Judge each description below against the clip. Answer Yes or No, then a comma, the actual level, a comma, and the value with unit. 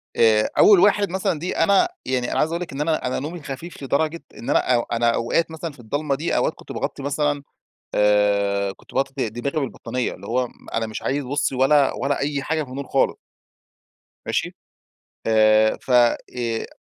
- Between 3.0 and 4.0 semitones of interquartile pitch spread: No, average, 4.7 semitones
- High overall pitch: No, low, 135 Hz